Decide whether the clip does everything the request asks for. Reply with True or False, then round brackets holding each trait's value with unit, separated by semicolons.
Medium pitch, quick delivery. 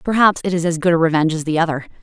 True (170 Hz; 295 wpm)